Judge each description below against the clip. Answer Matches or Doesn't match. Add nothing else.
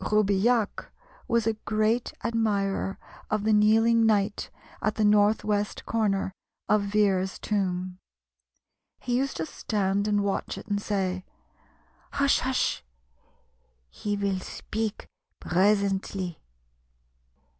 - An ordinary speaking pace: Doesn't match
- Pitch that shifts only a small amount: Matches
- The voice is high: Matches